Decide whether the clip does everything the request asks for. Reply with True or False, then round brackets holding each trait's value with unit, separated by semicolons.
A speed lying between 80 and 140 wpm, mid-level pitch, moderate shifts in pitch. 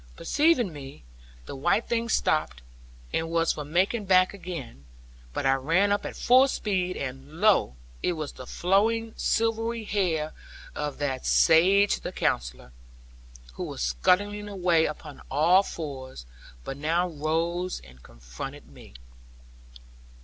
False (135 wpm; 170 Hz; 6.3 semitones)